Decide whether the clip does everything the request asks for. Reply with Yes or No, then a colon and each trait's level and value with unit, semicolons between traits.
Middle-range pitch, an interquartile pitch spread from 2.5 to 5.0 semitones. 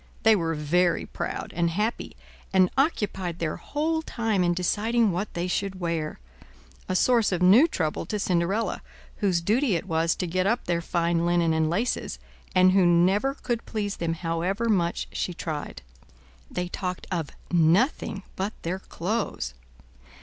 Yes: medium, 180 Hz; average, 3.8 semitones